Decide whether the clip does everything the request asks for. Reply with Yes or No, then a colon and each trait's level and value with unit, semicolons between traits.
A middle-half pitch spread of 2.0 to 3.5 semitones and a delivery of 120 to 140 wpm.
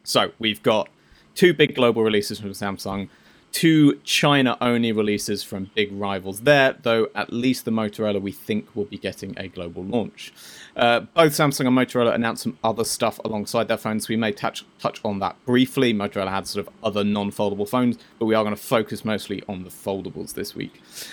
No: average, 3.2 semitones; average, 190 wpm